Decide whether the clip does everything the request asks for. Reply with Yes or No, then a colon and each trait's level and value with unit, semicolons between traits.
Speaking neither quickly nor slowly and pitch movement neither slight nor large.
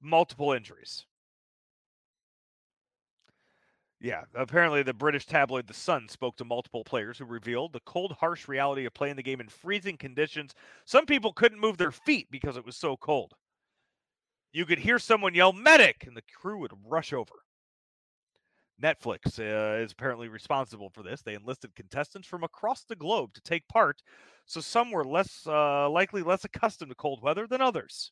No: average, 170 wpm; wide, 6.8 semitones